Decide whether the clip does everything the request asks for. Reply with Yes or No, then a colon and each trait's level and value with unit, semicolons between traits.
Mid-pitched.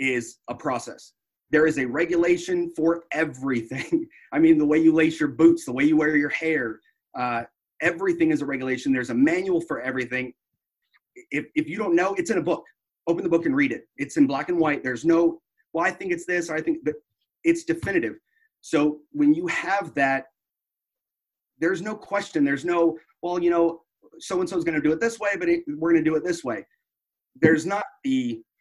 Yes: medium, 170 Hz